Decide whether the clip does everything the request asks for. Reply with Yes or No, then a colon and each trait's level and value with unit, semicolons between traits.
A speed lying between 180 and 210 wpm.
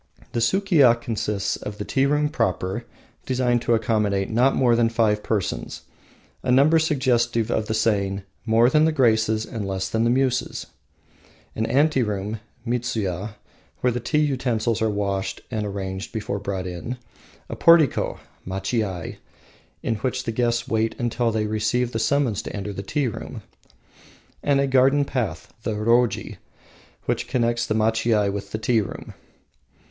No: average, 155 wpm